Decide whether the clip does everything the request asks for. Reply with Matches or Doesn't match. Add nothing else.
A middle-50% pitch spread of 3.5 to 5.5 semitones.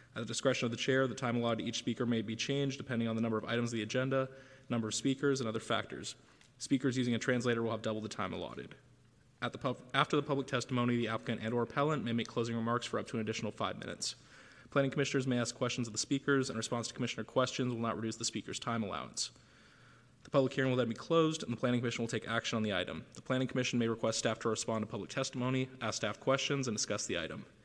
Doesn't match